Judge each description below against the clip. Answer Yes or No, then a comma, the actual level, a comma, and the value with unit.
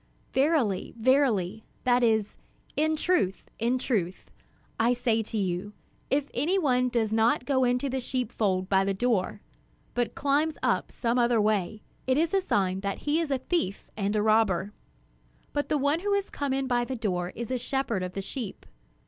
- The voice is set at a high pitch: Yes, high, 240 Hz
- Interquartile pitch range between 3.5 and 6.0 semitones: Yes, average, 4.7 semitones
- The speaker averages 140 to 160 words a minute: No, average, 180 wpm